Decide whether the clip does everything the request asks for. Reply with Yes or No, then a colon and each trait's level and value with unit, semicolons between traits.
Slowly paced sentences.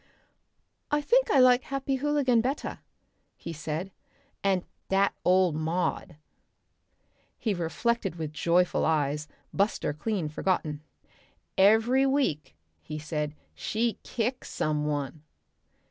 Yes: slow, 110 wpm